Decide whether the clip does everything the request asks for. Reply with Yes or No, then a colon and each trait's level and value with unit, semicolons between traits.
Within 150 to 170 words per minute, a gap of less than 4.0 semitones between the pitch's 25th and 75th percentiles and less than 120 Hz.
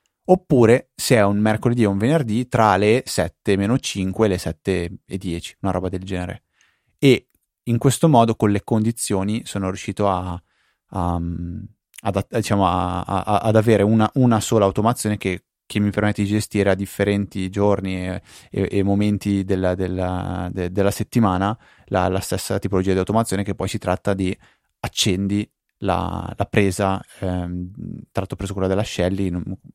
Yes: average, 160 wpm; narrow, 2.5 semitones; low, 100 Hz